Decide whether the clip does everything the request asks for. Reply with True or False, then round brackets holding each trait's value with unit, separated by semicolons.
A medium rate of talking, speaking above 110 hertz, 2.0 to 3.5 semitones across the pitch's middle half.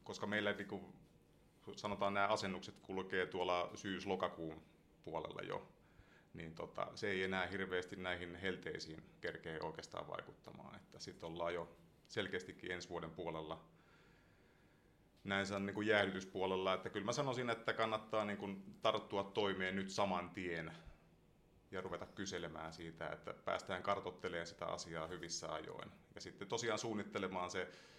False (135 wpm; 95 Hz; 2.4 semitones)